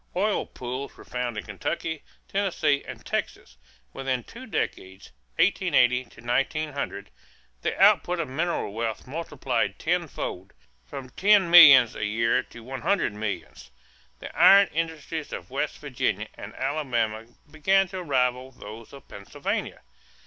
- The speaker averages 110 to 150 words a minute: Yes, slow, 135 wpm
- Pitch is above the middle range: No, low, 135 Hz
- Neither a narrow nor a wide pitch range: No, wide, 6.2 semitones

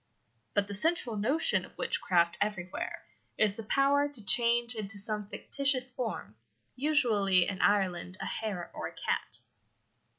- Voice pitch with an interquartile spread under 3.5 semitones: No, average, 4.4 semitones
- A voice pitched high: Yes, high, 215 Hz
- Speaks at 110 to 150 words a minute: Yes, average, 140 wpm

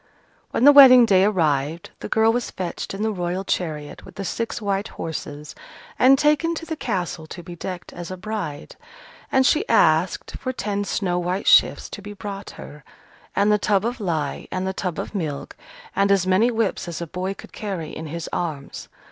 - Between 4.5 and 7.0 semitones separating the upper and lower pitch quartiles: No, average, 4.1 semitones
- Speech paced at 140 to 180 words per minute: No, average, 200 wpm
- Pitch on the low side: No, high, 190 Hz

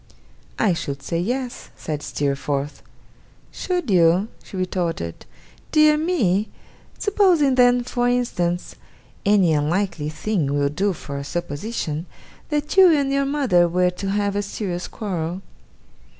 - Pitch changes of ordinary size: No, wide, 7.1 semitones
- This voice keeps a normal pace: No, slow, 130 wpm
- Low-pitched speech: No, high, 195 Hz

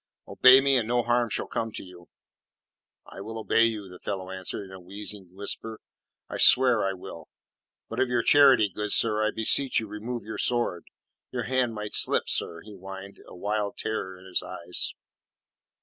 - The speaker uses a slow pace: No, average, 185 wpm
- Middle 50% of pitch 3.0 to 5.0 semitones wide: Yes, average, 3.5 semitones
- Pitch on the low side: Yes, low, 105 Hz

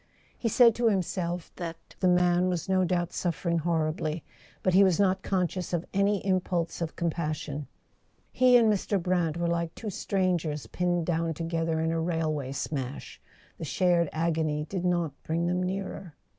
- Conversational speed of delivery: Yes, average, 170 wpm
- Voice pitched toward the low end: No, medium, 175 Hz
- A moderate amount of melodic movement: No, narrow, 2.3 semitones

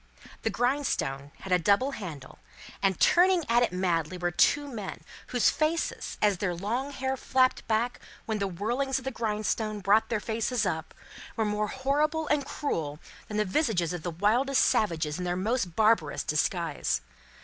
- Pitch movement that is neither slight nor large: No, wide, 6.4 semitones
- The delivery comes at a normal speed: Yes, average, 170 wpm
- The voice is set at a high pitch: Yes, high, 215 Hz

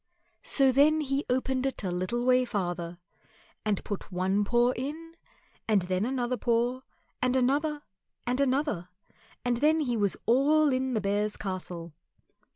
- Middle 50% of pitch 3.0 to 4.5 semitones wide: No, average, 5.0 semitones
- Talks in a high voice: Yes, high, 245 Hz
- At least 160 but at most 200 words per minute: No, average, 150 wpm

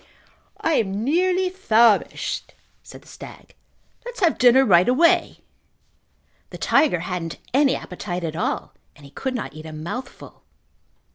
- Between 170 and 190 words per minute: No, average, 140 wpm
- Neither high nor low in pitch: No, high, 235 Hz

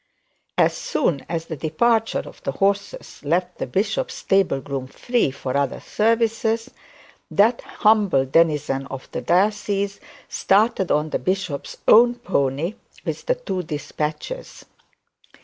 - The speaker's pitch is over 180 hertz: Yes, high, 190 Hz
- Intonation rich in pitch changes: Yes, wide, 6.8 semitones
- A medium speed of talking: No, slow, 130 wpm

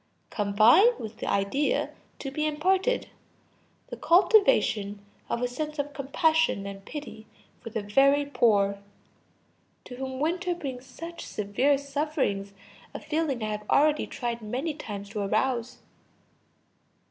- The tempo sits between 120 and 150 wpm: Yes, slow, 135 wpm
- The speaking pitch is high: Yes, very high, 265 Hz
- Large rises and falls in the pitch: Yes, wide, 6.2 semitones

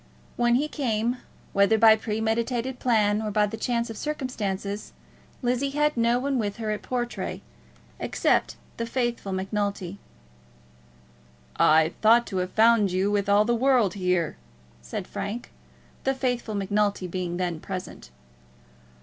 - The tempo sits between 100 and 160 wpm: Yes, average, 140 wpm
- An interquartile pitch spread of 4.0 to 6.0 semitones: No, average, 3.2 semitones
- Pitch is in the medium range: No, high, 220 Hz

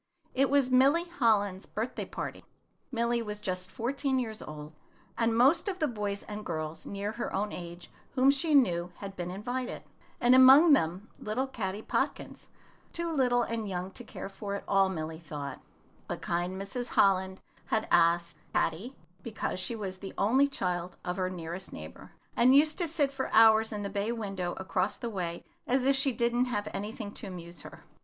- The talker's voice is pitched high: Yes, high, 210 Hz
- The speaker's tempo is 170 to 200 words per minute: Yes, average, 185 wpm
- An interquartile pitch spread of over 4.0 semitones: Yes, wide, 5.5 semitones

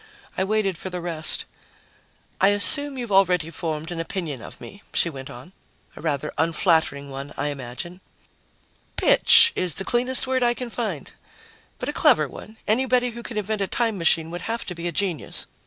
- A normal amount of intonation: No, wide, 5.9 semitones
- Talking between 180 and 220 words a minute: Yes, average, 185 wpm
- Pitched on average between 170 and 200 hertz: Yes, medium, 185 Hz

